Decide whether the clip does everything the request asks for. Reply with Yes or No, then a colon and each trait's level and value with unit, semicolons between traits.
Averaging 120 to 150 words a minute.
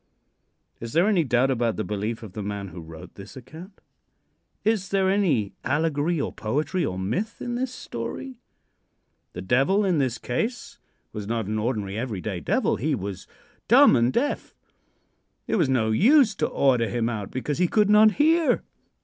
No: average, 175 wpm